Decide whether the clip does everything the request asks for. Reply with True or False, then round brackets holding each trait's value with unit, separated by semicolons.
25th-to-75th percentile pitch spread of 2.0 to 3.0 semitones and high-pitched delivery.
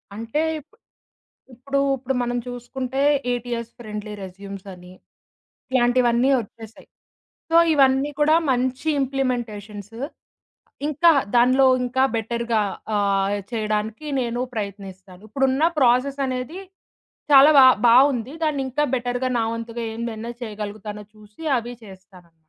False (3.7 semitones; 235 Hz)